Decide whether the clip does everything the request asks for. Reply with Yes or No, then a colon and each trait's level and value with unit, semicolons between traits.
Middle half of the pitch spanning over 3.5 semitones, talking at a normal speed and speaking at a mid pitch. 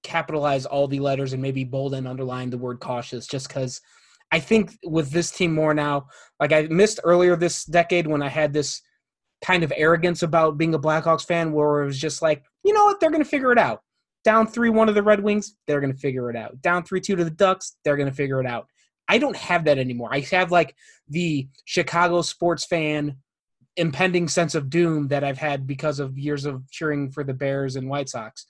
No: average, 3.9 semitones; fast, 225 wpm; medium, 155 Hz